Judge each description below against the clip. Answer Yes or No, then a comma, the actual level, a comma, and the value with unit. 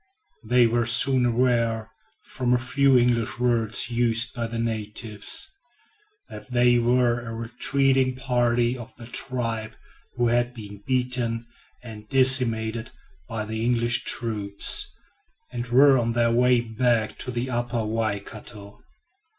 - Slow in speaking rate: Yes, slow, 130 wpm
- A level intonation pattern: Yes, narrow, 1.6 semitones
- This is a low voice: Yes, low, 120 Hz